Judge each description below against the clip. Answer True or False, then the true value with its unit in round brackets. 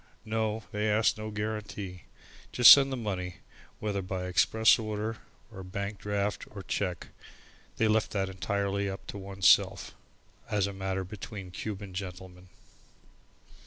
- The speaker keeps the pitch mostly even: True (2.2 semitones)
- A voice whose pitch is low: True (100 Hz)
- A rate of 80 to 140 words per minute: True (135 wpm)